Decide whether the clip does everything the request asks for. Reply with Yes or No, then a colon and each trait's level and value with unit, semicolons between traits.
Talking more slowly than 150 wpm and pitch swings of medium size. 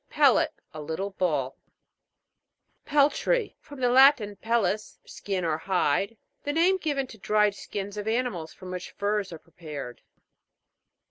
No: average, 140 wpm; wide, 5.9 semitones